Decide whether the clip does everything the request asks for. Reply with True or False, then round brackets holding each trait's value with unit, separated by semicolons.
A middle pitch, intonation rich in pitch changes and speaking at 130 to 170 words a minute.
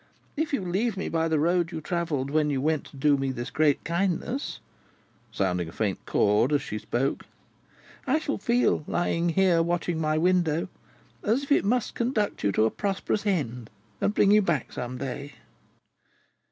False (165 Hz; 6.1 semitones; 180 wpm)